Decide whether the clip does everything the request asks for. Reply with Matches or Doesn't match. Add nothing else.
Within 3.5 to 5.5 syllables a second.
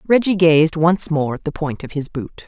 Matches